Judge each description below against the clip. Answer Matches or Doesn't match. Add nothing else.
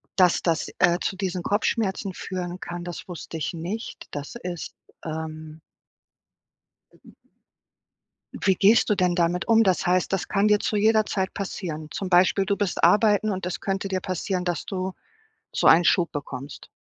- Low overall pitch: Doesn't match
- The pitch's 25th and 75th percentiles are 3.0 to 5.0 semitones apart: Doesn't match